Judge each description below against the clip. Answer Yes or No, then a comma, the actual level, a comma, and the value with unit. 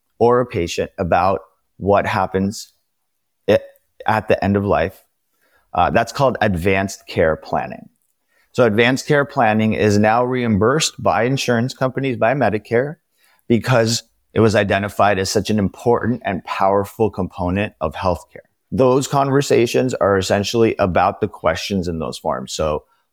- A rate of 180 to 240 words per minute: No, average, 140 wpm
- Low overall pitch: Yes, low, 110 Hz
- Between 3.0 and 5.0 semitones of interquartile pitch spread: Yes, average, 3.9 semitones